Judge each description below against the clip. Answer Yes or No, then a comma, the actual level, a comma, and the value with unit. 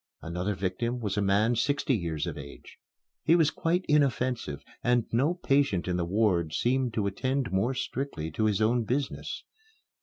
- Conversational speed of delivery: Yes, average, 170 wpm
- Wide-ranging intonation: Yes, wide, 6.0 semitones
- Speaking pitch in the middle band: No, low, 115 Hz